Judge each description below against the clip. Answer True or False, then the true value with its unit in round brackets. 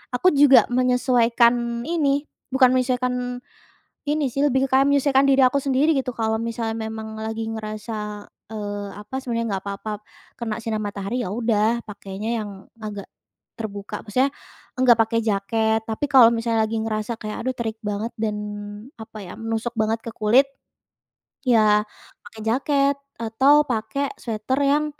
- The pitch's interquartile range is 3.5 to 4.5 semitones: False (3.0 semitones)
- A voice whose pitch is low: False (230 Hz)